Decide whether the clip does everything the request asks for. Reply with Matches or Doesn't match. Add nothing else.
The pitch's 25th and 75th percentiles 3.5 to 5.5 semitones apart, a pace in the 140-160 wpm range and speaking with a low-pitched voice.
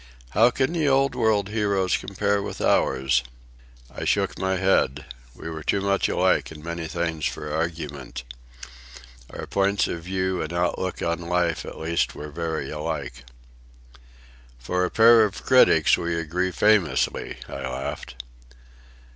Matches